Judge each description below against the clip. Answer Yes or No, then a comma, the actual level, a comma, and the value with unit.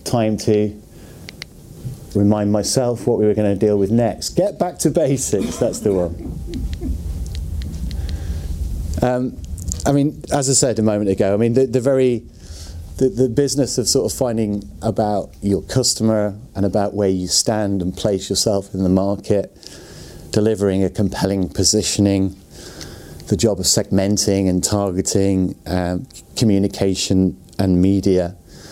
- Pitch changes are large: No, average, 3.3 semitones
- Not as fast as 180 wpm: Yes, average, 140 wpm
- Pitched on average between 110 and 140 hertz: No, low, 100 Hz